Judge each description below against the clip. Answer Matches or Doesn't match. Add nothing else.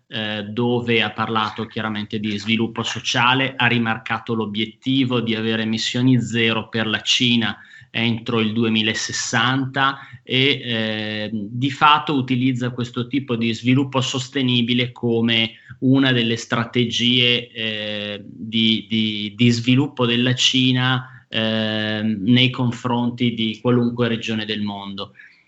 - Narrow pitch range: Matches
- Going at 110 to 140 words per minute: Matches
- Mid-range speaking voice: Doesn't match